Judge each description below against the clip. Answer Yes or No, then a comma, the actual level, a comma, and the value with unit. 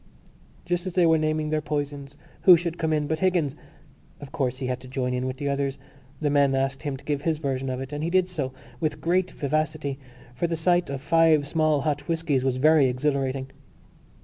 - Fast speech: Yes, fast, 215 wpm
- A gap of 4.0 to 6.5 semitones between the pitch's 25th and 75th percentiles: No, average, 3.1 semitones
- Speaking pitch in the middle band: Yes, medium, 145 Hz